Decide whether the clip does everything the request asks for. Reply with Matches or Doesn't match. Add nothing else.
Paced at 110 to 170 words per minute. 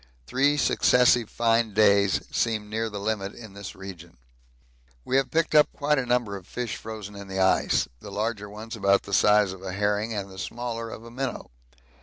Doesn't match